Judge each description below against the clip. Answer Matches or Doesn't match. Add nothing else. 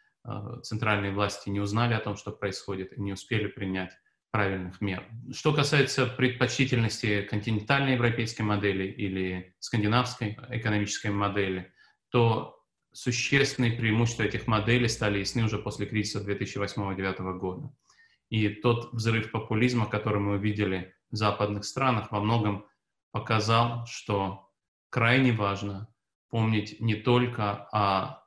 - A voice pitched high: Doesn't match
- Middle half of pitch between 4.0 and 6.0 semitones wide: Doesn't match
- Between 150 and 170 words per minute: Doesn't match